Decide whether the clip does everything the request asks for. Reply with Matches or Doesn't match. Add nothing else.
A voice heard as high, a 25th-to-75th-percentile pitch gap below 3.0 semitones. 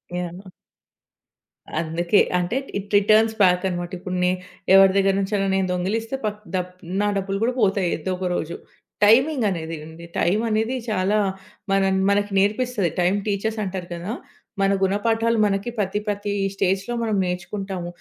Matches